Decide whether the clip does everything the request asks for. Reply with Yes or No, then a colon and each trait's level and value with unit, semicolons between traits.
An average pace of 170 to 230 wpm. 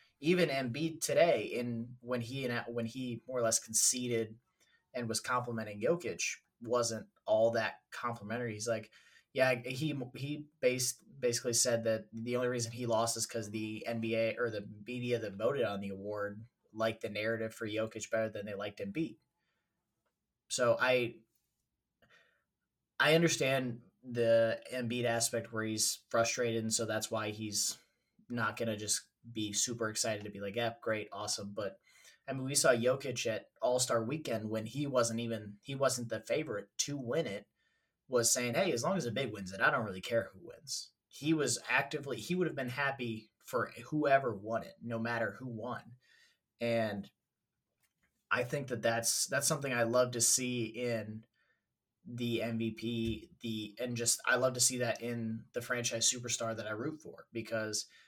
Yes: average, 175 wpm